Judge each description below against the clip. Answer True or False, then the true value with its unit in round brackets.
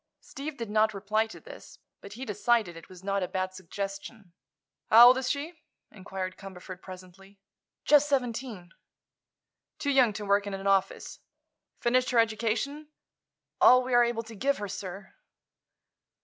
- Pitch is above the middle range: True (215 Hz)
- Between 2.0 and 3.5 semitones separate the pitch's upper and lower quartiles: False (4.3 semitones)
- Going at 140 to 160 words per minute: True (155 wpm)